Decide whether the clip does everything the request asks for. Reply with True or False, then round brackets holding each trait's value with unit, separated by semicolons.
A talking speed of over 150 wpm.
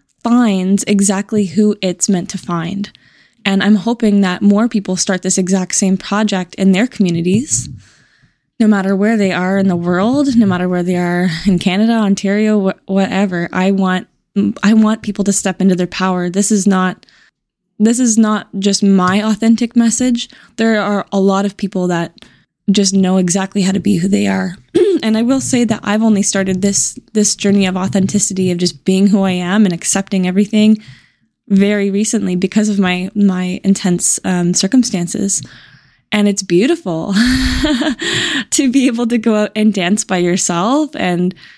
True (175 wpm)